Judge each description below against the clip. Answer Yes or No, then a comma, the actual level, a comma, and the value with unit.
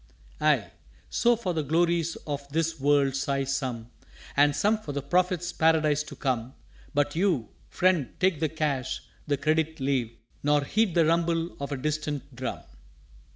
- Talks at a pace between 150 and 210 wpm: Yes, average, 155 wpm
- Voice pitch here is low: No, medium, 150 Hz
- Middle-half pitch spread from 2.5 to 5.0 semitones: Yes, average, 3.1 semitones